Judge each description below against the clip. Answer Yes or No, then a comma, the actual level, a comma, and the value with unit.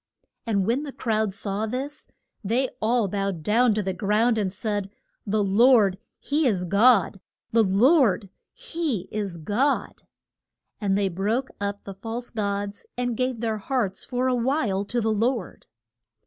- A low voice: No, high, 215 Hz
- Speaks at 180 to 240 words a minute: No, average, 155 wpm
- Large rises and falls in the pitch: No, average, 3.8 semitones